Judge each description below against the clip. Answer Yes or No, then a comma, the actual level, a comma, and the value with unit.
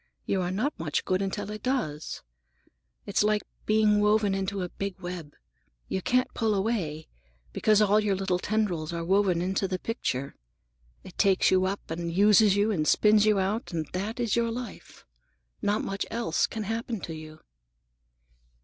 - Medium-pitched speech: No, high, 200 Hz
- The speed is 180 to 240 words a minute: No, average, 170 wpm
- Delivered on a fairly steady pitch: No, average, 3.0 semitones